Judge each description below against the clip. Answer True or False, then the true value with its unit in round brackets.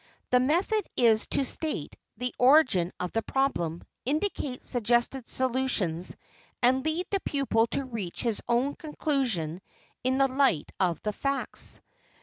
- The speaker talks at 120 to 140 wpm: True (135 wpm)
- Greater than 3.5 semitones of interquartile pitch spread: True (4.2 semitones)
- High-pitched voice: True (255 Hz)